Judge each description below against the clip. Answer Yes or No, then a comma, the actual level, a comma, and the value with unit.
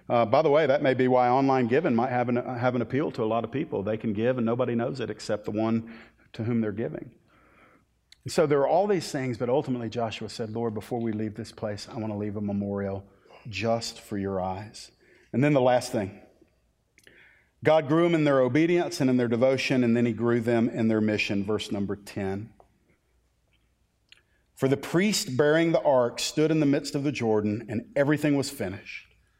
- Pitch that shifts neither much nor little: Yes, average, 3.7 semitones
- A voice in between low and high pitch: No, low, 115 Hz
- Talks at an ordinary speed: No, fast, 215 wpm